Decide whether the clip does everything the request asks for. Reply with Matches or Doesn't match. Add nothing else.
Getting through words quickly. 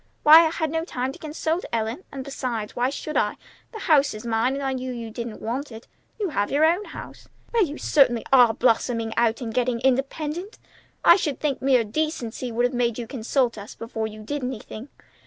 Matches